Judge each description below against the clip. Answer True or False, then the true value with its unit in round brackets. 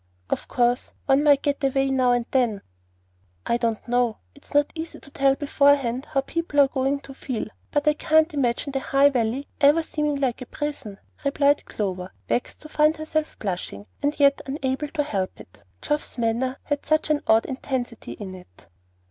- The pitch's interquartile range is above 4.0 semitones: False (3.5 semitones)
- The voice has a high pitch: True (270 Hz)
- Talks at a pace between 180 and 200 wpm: True (185 wpm)